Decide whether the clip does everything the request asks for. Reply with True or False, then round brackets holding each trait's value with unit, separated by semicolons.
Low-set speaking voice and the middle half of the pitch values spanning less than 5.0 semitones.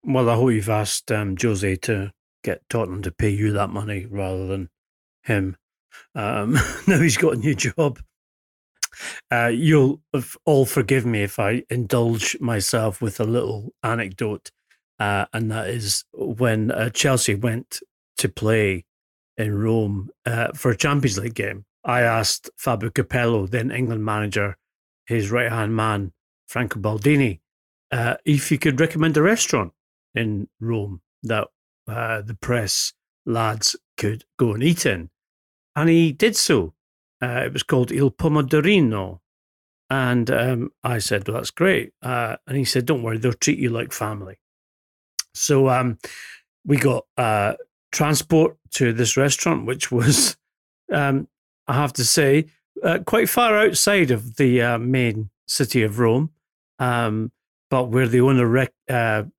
True (120 Hz; 4.2 semitones)